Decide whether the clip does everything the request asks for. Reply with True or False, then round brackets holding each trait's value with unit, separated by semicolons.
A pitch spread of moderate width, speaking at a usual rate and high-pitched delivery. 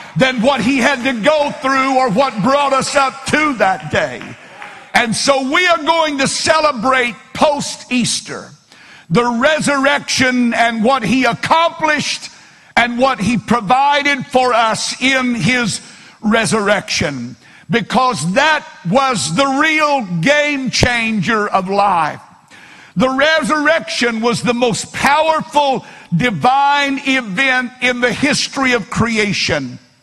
False (3.9 semitones; 120 wpm; 255 Hz)